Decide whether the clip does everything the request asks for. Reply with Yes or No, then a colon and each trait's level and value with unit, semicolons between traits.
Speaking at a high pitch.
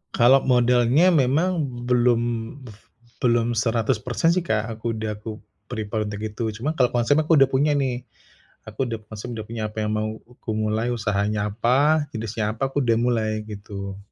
No: low, 115 Hz